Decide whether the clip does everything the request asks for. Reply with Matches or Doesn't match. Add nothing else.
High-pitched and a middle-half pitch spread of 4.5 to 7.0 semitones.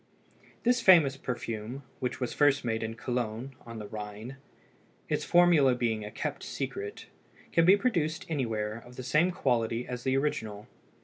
Doesn't match